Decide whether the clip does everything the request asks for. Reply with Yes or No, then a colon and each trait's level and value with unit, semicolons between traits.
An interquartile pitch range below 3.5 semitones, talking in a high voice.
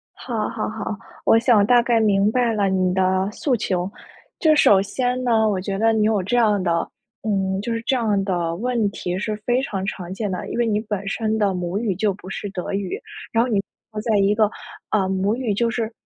Yes: average, 2.9 semitones; high, 210 Hz